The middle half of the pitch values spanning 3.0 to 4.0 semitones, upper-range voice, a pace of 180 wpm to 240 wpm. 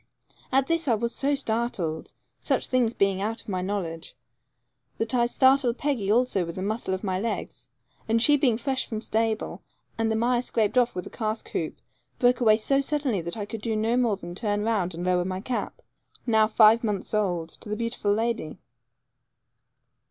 Yes: average, 3.5 semitones; high, 220 Hz; average, 190 wpm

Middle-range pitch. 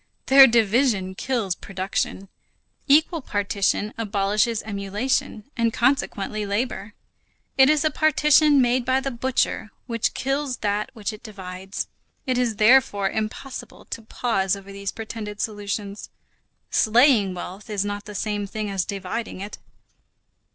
No: high, 215 Hz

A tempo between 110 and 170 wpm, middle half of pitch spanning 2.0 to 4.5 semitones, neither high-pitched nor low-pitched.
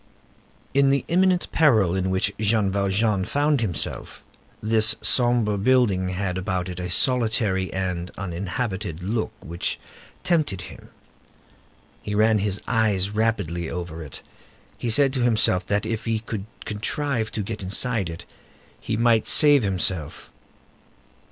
No: slow, 135 wpm; average, 3.8 semitones; low, 105 Hz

